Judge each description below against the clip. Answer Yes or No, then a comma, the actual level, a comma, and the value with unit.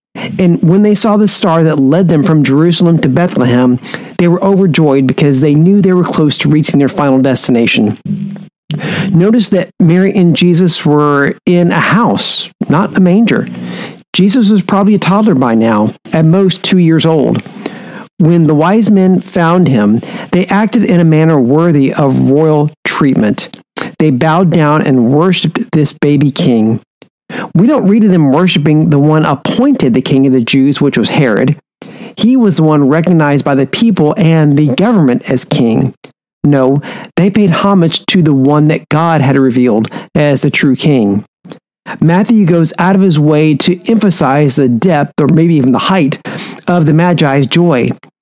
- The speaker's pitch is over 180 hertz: No, medium, 165 Hz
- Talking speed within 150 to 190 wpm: Yes, average, 170 wpm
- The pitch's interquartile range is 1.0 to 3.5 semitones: No, average, 4.7 semitones